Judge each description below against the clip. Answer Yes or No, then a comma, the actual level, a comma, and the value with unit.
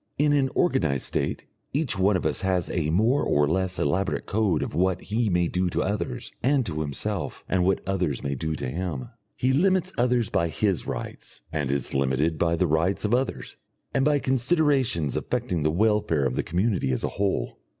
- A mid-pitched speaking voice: No, very low, 95 Hz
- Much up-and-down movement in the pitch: Yes, wide, 7.2 semitones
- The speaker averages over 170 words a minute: Yes, average, 195 wpm